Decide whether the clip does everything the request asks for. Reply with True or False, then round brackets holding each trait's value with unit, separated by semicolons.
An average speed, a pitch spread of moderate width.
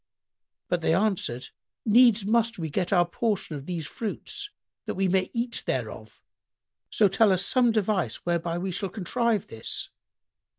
True (155 wpm; 4.6 semitones)